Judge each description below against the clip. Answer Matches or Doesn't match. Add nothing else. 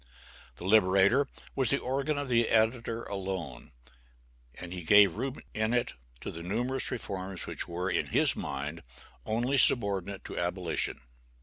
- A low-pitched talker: Matches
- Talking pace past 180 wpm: Doesn't match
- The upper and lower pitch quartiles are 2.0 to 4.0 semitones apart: Doesn't match